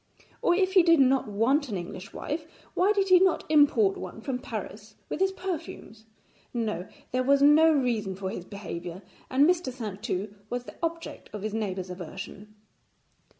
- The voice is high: Yes, high, 245 Hz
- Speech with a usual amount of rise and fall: No, wide, 7.6 semitones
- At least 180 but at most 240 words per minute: No, average, 170 wpm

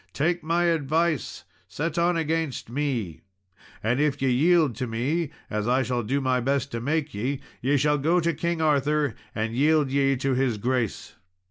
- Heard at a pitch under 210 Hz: Yes, medium, 140 Hz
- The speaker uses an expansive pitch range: No, average, 4.1 semitones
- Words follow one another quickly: No, average, 175 wpm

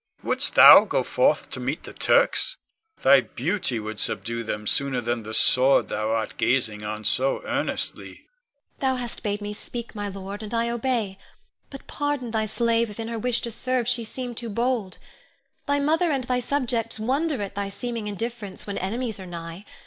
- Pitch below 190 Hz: No, high, 220 Hz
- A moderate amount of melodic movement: No, wide, 5.7 semitones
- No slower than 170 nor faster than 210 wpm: Yes, average, 185 wpm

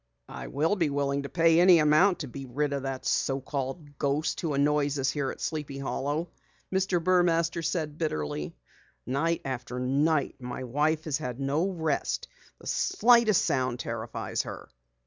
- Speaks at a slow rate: No, average, 160 wpm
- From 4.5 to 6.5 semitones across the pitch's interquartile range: No, average, 3.5 semitones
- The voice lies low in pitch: No, medium, 145 Hz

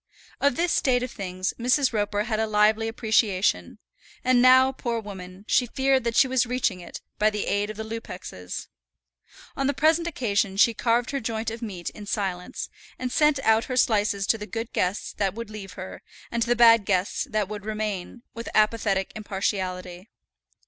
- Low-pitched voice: No, high, 220 Hz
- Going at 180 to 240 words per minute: Yes, average, 185 wpm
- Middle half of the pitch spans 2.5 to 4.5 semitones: Yes, average, 3.3 semitones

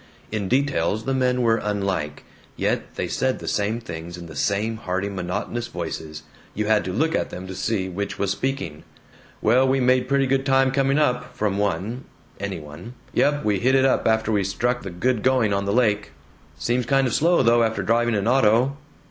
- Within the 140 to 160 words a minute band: No, average, 200 wpm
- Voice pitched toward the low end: Yes, low, 110 Hz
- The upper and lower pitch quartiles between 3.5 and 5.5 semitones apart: Yes, average, 4.7 semitones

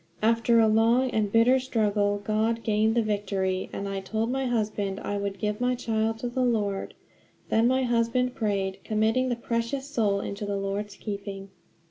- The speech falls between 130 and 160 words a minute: No, average, 175 wpm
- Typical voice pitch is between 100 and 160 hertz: No, high, 220 Hz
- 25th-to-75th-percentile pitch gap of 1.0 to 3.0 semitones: Yes, average, 2.7 semitones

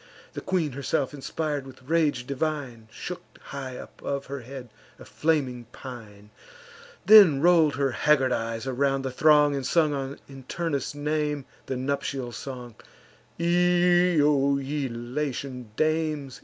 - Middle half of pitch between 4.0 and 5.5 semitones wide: No, average, 2.9 semitones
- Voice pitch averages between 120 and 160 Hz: Yes, medium, 140 Hz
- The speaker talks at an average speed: No, slow, 130 wpm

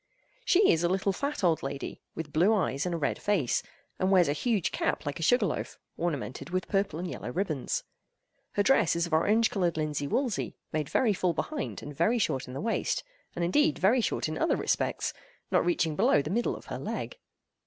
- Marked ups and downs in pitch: Yes, wide, 6.0 semitones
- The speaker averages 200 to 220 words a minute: Yes, fast, 205 wpm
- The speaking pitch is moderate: Yes, medium, 180 Hz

